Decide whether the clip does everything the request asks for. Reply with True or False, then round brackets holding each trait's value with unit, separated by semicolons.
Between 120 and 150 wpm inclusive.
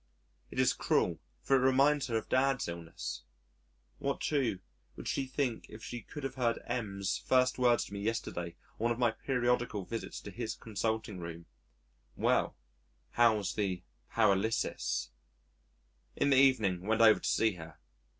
False (160 wpm)